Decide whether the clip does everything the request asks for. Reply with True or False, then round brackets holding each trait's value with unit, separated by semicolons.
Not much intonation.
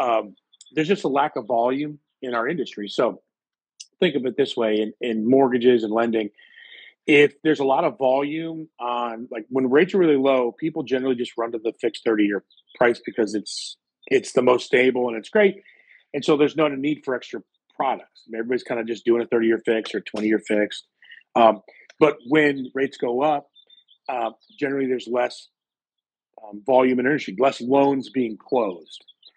False (3.9 semitones)